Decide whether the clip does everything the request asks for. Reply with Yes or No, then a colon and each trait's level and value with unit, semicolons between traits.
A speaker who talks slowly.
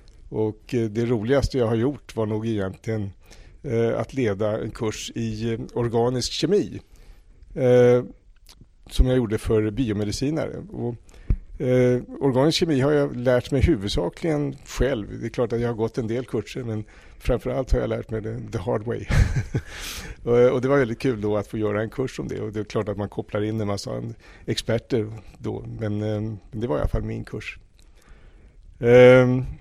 No: average, 185 wpm